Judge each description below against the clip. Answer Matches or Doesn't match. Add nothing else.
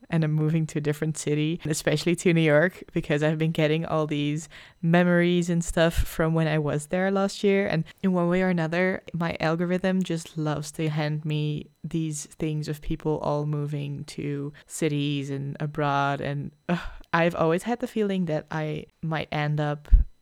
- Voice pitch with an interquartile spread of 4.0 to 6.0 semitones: Doesn't match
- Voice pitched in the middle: Matches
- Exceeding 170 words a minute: Matches